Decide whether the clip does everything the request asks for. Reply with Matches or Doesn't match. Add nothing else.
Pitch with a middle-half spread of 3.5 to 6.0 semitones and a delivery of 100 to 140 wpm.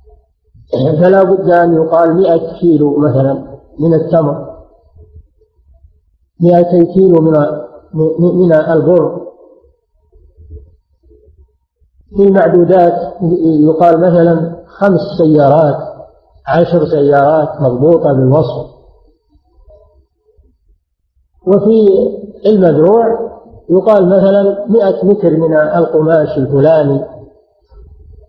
Doesn't match